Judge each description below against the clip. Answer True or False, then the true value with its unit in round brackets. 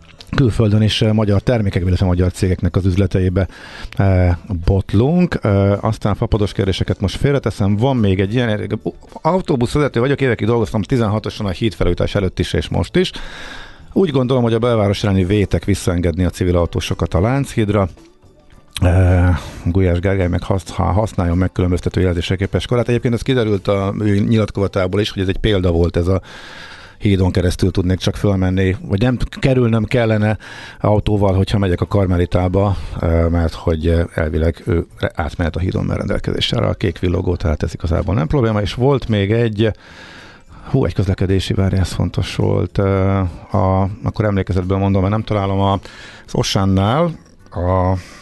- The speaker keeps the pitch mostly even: False (3.3 semitones)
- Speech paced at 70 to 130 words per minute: False (155 wpm)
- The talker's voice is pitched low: True (100 Hz)